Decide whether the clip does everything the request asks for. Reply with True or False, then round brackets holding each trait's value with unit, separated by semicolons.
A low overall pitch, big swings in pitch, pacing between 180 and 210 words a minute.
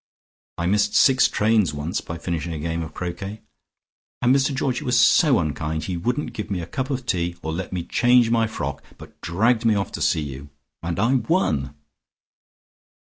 True (95 Hz; 6.7 semitones; 185 wpm)